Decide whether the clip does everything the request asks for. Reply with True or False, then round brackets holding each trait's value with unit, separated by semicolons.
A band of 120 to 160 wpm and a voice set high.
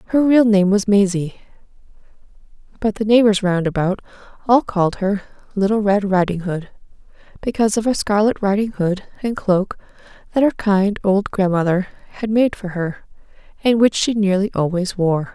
True (155 wpm; 200 Hz)